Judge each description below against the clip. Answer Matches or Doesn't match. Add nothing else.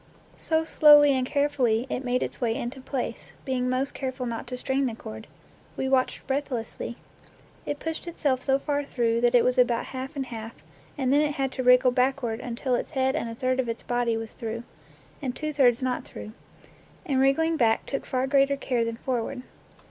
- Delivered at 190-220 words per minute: Matches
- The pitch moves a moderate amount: Doesn't match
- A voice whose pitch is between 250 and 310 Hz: Matches